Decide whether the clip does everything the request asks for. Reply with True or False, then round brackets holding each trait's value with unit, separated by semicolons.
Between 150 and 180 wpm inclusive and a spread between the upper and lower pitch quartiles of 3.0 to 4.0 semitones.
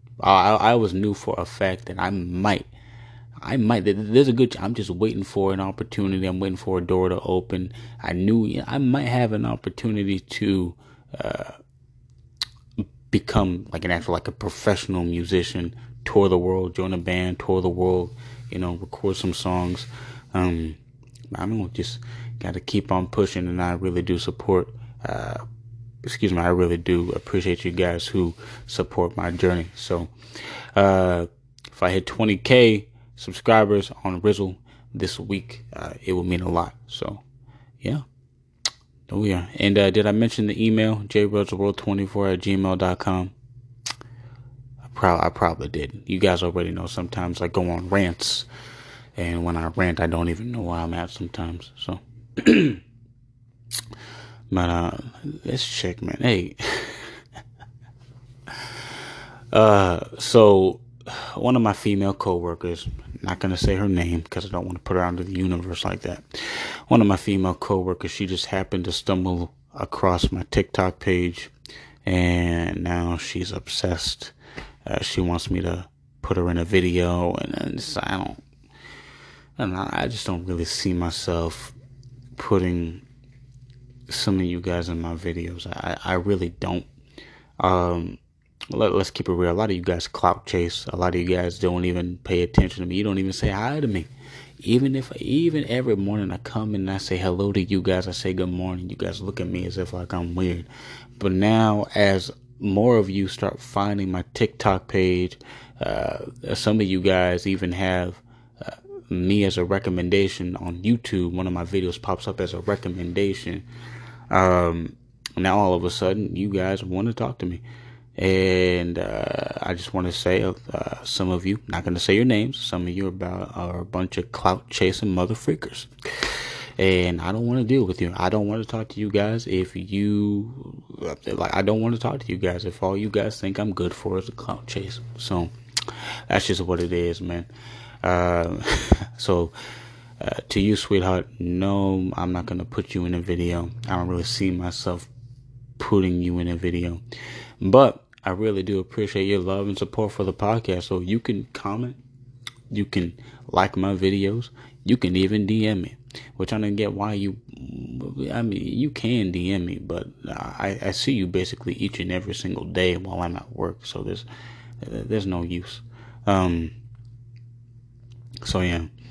False (175 wpm; 4.6 semitones)